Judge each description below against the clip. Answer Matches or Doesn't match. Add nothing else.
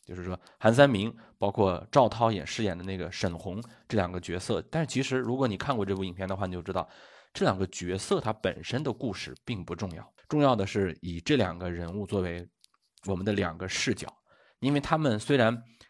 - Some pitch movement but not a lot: Matches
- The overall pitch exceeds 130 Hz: Doesn't match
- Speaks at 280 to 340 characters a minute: Matches